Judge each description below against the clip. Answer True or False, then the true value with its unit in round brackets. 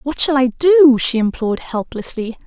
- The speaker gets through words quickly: False (170 wpm)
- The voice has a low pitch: False (260 Hz)